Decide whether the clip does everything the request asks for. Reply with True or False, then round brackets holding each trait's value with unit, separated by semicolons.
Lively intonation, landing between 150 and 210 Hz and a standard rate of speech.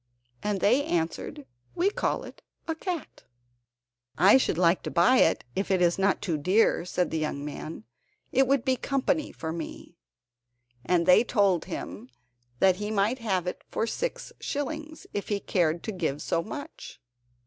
True (7.3 semitones; 190 Hz; 165 wpm)